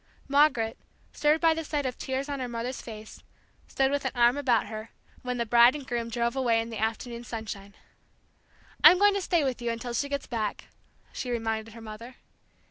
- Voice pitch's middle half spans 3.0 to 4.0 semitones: Yes, average, 3.4 semitones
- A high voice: Yes, high, 240 Hz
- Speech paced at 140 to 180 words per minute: No, average, 200 wpm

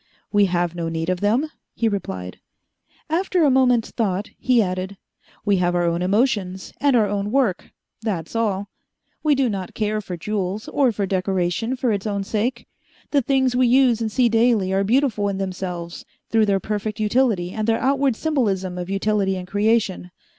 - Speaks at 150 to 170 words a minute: No, average, 180 wpm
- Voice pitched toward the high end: Yes, high, 210 Hz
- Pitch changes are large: No, average, 4.2 semitones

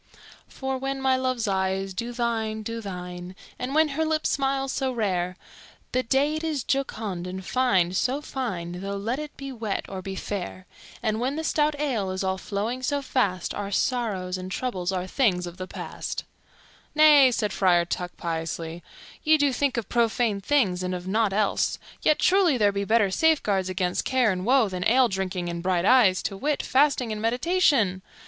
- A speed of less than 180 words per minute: No, average, 185 wpm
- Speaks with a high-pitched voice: Yes, high, 220 Hz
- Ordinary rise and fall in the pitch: No, wide, 6.0 semitones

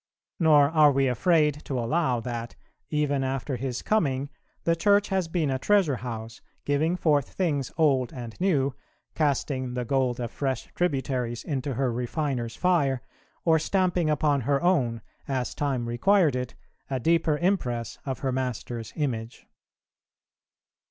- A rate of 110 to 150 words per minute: Yes, average, 145 wpm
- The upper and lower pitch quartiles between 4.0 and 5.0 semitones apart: Yes, average, 4.3 semitones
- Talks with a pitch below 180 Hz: Yes, medium, 140 Hz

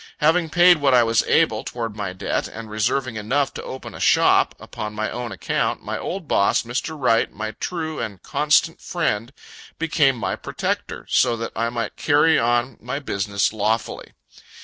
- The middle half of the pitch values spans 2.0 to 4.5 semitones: No, wide, 5.5 semitones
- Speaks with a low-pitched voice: Yes, low, 120 Hz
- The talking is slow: No, average, 170 wpm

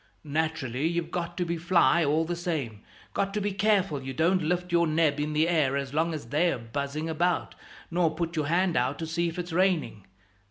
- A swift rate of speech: Yes, fast, 210 wpm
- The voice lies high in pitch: No, medium, 165 Hz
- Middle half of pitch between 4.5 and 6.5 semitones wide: No, average, 2.8 semitones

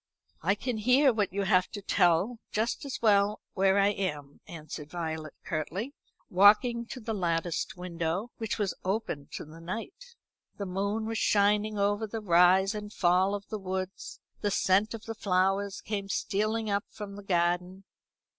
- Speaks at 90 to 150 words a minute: No, average, 165 wpm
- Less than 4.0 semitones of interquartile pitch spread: Yes, average, 3.0 semitones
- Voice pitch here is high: Yes, high, 200 Hz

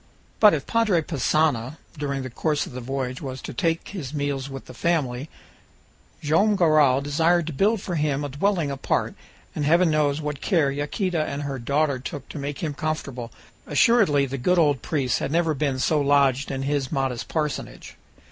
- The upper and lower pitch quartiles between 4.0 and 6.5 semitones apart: No, average, 2.9 semitones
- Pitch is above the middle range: No, medium, 145 Hz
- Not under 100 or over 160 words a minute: No, average, 185 wpm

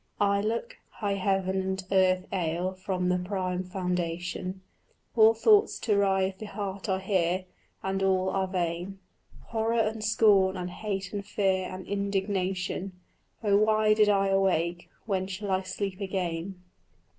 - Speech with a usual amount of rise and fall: No, narrow, 1.6 semitones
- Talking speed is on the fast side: No, average, 145 wpm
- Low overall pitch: No, high, 190 Hz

